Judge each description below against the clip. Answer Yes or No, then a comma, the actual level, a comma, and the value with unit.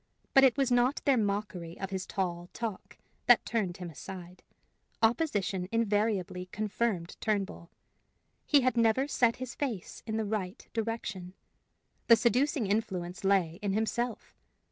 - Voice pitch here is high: Yes, high, 210 Hz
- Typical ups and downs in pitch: Yes, average, 4.1 semitones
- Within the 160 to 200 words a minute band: No, average, 140 wpm